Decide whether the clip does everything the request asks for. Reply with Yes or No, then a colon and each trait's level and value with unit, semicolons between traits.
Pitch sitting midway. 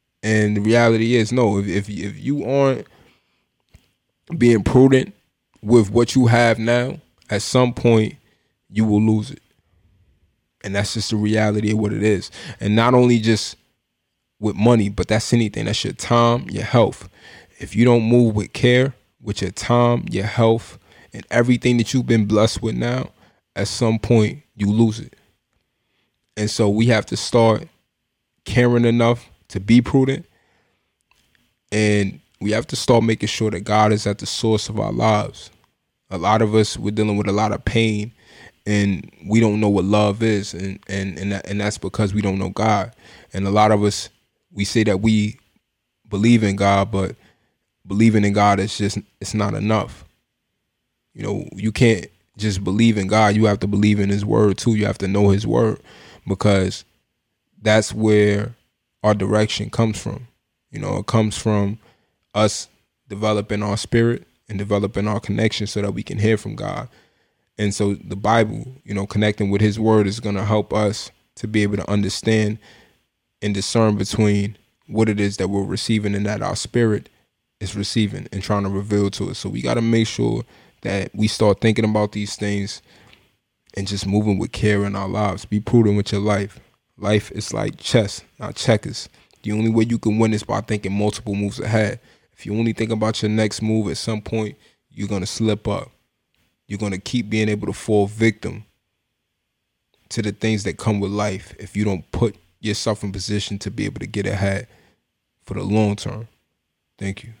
No: low, 105 Hz